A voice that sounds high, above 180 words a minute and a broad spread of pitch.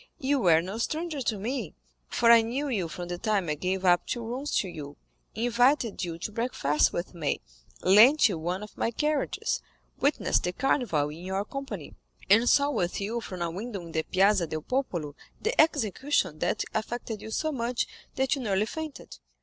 Yes: high, 215 Hz; average, 190 wpm; wide, 6.5 semitones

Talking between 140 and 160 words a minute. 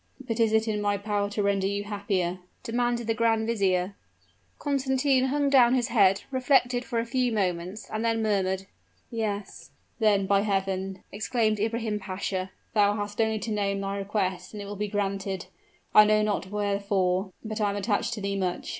No: average, 180 wpm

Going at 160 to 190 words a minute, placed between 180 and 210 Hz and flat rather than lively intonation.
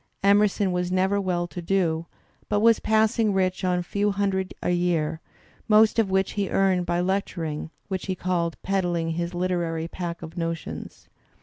Yes: average, 170 wpm; medium, 185 Hz; narrow, 2.3 semitones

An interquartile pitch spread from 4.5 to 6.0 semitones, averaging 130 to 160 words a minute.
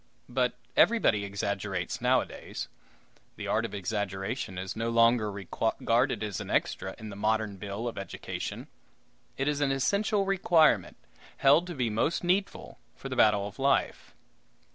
Yes: wide, 5.5 semitones; average, 145 wpm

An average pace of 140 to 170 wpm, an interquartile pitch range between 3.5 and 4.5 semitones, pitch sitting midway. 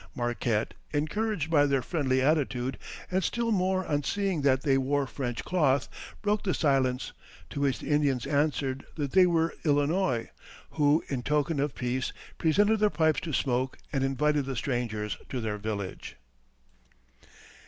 Yes: average, 155 wpm; average, 3.8 semitones; medium, 145 Hz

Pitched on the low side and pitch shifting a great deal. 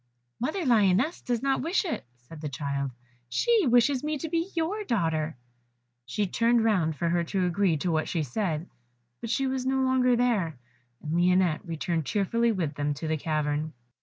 No: high, 190 Hz; wide, 8.2 semitones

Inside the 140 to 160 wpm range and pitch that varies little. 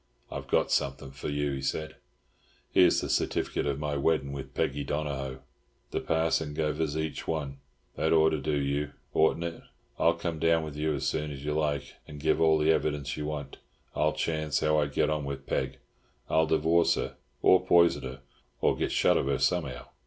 No: average, 195 wpm; narrow, 2.1 semitones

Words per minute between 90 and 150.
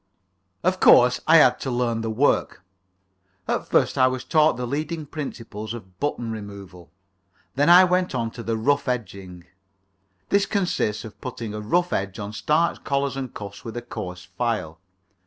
No: average, 170 wpm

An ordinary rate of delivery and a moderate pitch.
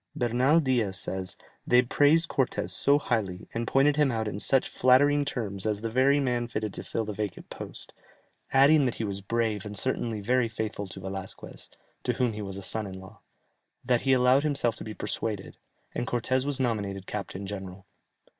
No: average, 185 wpm; low, 115 Hz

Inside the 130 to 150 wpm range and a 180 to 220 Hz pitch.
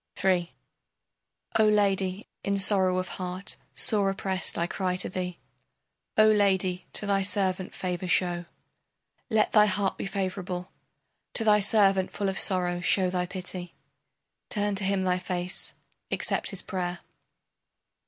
Yes: average, 140 wpm; high, 190 Hz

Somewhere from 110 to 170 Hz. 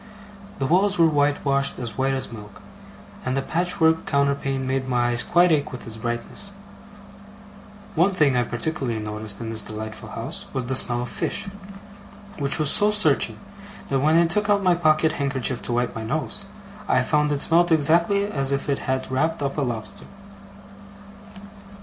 Yes: medium, 140 Hz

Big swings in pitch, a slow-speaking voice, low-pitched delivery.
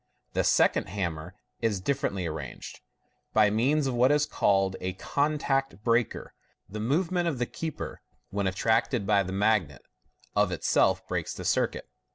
No: wide, 5.9 semitones; average, 160 wpm; low, 110 Hz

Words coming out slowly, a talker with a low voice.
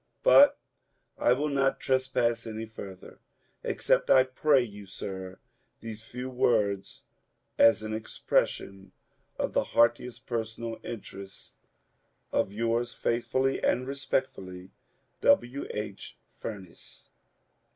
Yes: slow, 105 wpm; low, 115 Hz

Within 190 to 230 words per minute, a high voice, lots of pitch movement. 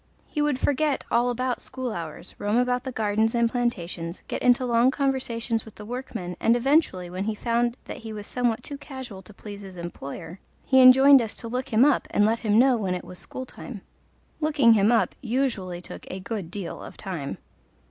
No: fast, 205 wpm; high, 230 Hz; average, 4.2 semitones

